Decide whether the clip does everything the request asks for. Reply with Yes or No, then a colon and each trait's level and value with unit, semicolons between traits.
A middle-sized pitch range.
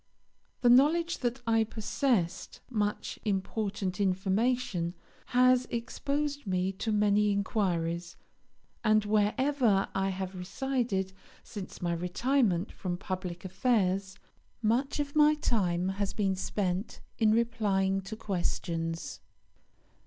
Yes: average, 4.2 semitones